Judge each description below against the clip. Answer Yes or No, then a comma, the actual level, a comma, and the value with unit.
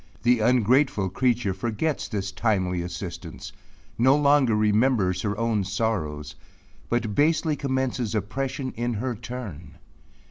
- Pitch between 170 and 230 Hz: No, low, 115 Hz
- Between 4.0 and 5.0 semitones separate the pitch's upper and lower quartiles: Yes, average, 4.5 semitones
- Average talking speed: No, slow, 115 wpm